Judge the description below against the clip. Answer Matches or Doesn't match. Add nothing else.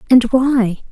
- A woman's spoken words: Matches